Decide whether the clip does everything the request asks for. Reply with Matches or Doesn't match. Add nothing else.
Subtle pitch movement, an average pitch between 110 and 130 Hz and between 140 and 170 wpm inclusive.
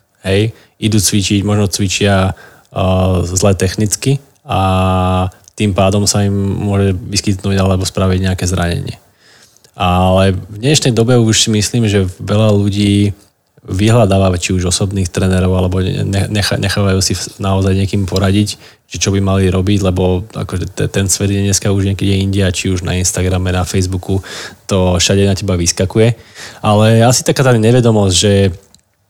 Doesn't match